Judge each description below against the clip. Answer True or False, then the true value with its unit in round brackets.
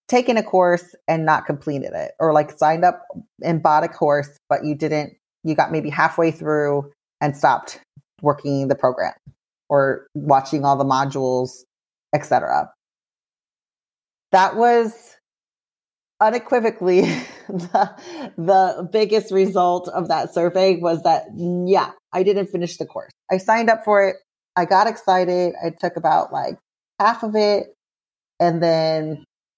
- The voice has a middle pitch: True (175 Hz)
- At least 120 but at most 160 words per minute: True (140 wpm)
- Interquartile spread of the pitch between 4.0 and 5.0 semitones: True (4.5 semitones)